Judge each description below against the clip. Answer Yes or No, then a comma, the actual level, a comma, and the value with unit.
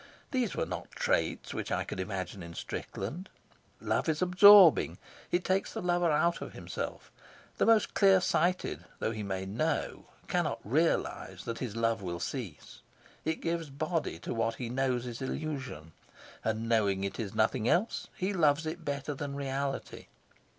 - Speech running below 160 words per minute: No, average, 165 wpm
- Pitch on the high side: No, medium, 140 Hz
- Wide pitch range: Yes, wide, 7.3 semitones